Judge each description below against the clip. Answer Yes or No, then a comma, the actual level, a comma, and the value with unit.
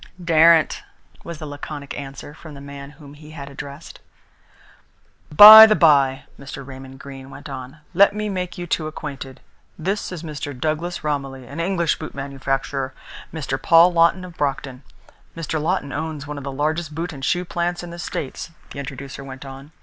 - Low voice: No, medium, 150 Hz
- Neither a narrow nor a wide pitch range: Yes, average, 3.4 semitones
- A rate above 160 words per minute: Yes, average, 175 wpm